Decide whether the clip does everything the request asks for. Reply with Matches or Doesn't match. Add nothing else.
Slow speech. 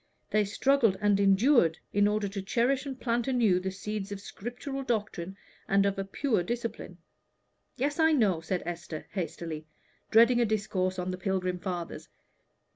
Doesn't match